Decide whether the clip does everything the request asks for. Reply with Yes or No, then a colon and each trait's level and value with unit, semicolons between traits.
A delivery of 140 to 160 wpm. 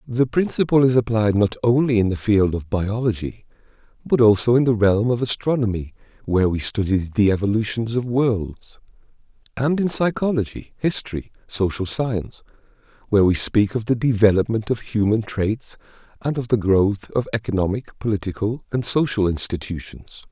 Yes: average, 150 wpm